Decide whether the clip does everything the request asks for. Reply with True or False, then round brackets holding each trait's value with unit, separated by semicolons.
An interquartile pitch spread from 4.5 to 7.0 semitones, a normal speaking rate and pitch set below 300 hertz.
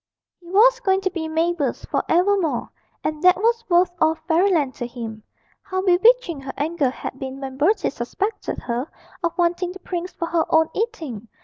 False (5.1 semitones; 180 wpm; 340 Hz)